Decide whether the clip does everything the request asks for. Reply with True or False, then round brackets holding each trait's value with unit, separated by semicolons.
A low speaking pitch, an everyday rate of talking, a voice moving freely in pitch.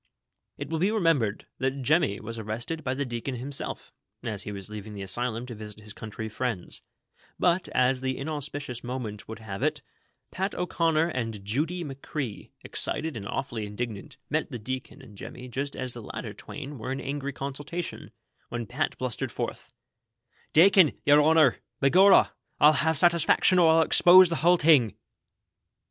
True (130 Hz; 170 wpm; 5.8 semitones)